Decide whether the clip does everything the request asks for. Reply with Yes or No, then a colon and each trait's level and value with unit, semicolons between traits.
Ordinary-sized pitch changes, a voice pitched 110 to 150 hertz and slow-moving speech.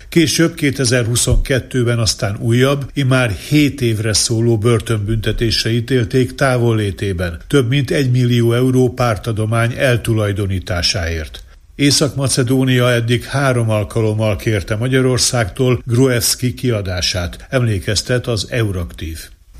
Yes: average, 3.3 semitones; low, 120 Hz; slow, 90 wpm